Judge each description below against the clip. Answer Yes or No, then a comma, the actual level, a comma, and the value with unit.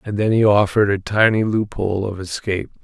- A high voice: No, low, 105 Hz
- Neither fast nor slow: Yes, average, 190 wpm